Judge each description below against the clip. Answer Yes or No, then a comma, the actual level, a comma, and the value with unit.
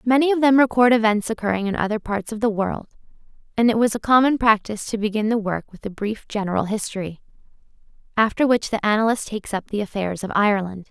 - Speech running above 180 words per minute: Yes, fast, 205 wpm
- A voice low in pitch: No, high, 215 Hz